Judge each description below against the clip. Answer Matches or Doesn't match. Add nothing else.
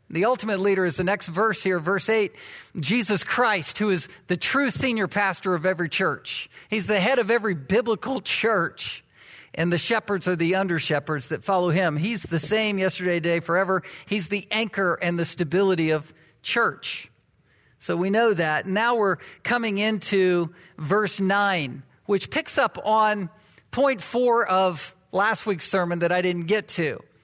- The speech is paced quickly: Doesn't match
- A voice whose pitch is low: Doesn't match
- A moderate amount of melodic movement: Matches